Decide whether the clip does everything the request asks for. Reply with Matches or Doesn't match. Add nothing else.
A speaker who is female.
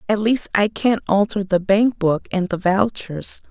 Matches